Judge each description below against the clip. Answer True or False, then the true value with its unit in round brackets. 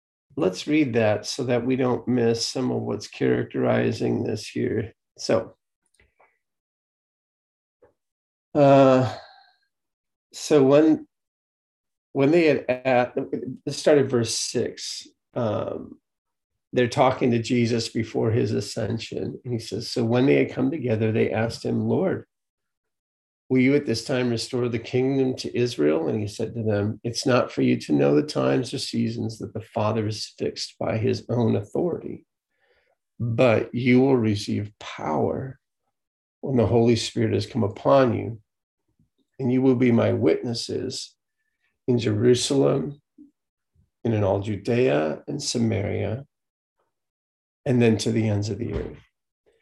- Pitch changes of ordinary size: True (3.3 semitones)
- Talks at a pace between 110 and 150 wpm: True (140 wpm)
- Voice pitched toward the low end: True (115 Hz)